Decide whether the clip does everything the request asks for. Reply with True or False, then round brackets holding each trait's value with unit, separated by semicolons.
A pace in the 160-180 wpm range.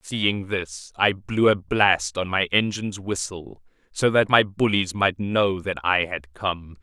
True (175 wpm)